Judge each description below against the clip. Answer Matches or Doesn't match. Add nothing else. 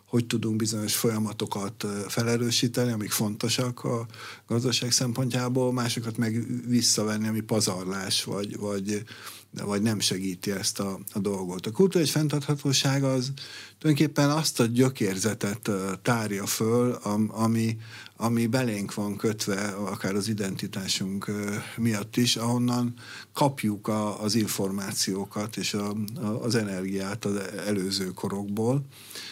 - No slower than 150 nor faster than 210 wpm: Doesn't match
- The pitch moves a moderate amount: Matches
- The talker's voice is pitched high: Doesn't match